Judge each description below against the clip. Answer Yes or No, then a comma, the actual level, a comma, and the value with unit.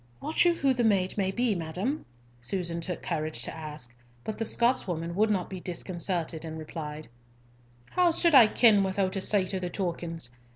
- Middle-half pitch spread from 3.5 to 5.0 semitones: Yes, average, 4.6 semitones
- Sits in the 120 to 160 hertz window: No, medium, 185 Hz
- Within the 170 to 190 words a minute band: Yes, average, 180 wpm